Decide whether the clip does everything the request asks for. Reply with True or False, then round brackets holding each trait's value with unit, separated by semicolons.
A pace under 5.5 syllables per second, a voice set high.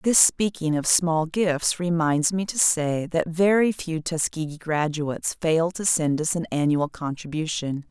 False (4.1 syllables/s; 160 Hz)